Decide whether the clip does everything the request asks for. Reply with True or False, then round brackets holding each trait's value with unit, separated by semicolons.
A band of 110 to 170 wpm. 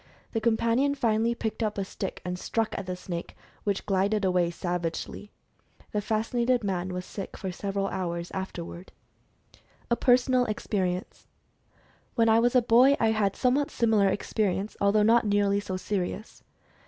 True (160 wpm)